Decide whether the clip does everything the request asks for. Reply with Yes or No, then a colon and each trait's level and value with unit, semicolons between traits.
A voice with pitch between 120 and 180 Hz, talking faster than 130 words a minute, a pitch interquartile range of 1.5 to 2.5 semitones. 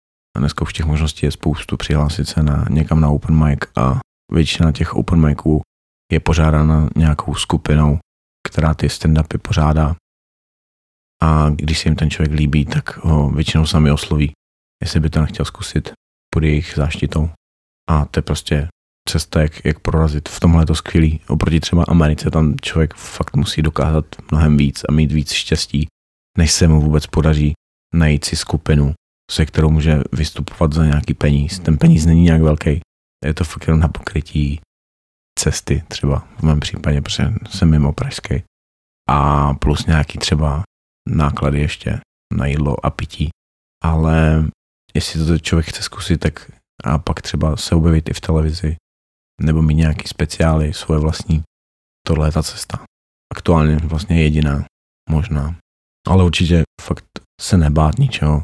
No: very low, 75 Hz; average, 155 wpm; narrow, 1.8 semitones